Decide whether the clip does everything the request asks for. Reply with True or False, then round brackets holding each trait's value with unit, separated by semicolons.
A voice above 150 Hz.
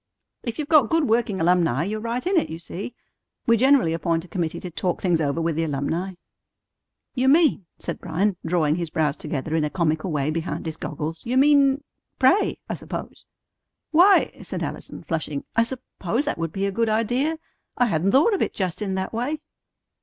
True (190 Hz)